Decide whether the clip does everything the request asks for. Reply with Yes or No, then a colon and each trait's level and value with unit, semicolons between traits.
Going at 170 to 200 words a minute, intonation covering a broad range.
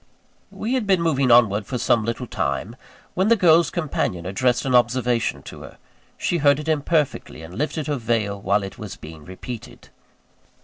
Yes: average, 175 wpm; wide, 6.9 semitones